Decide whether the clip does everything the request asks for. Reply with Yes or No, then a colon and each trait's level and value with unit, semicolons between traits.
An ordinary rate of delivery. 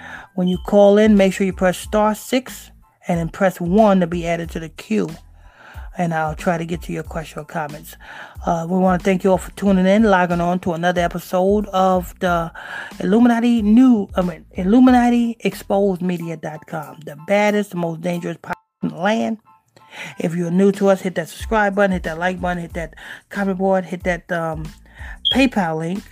Yes: average, 195 wpm